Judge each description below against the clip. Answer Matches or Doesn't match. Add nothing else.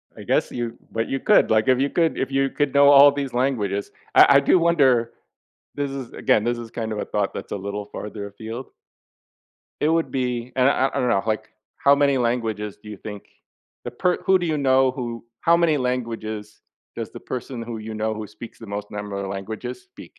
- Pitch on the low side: Matches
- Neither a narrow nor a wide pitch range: Matches